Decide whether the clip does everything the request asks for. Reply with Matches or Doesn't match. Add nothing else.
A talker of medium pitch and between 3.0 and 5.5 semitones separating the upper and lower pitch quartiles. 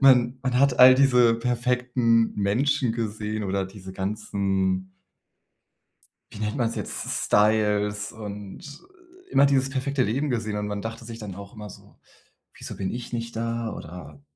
Doesn't match